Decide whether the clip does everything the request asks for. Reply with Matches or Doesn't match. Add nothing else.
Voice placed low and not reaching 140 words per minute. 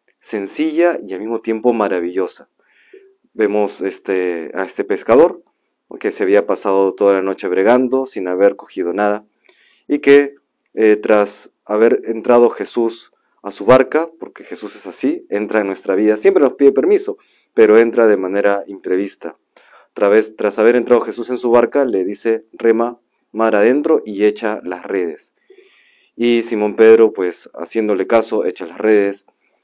Doesn't match